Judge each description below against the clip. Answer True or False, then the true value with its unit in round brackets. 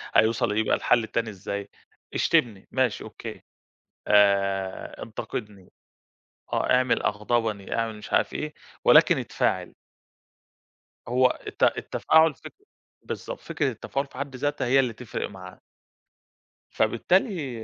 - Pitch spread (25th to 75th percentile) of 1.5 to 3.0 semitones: False (4.0 semitones)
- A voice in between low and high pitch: False (115 Hz)